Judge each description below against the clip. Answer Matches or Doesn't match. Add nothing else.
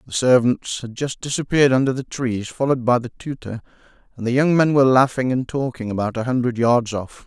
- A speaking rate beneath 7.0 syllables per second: Matches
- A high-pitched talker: Doesn't match